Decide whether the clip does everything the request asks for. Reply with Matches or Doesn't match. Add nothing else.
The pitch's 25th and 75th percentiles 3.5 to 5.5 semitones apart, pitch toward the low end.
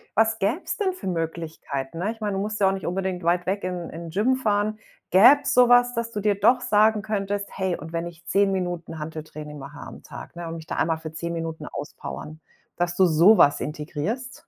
Doesn't match